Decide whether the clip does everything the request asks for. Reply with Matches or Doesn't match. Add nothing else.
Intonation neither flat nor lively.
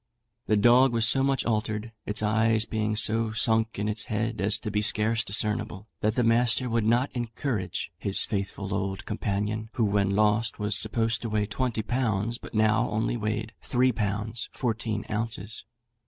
Doesn't match